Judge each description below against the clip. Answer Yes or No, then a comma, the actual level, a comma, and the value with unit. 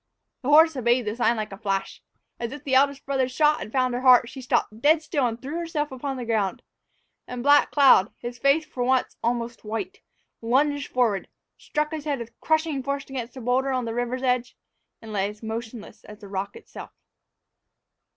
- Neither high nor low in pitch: No, very high, 250 Hz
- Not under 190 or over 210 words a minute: Yes, average, 200 wpm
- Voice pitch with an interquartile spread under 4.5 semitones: Yes, average, 3.6 semitones